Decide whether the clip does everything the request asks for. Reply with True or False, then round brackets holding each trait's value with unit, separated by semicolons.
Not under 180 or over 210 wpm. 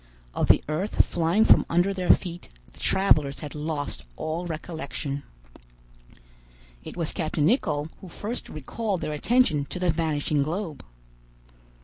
False (135 wpm)